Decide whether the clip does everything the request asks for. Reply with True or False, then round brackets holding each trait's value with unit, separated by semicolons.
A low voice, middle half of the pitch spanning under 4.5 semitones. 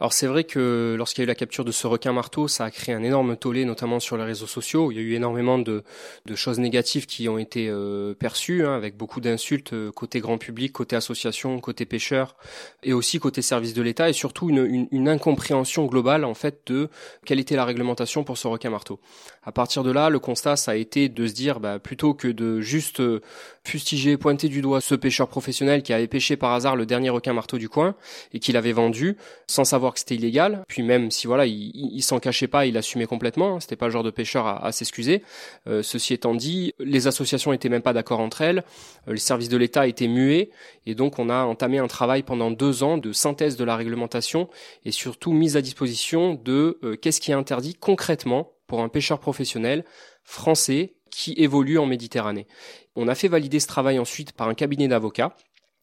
True (130 Hz; 3.4 semitones)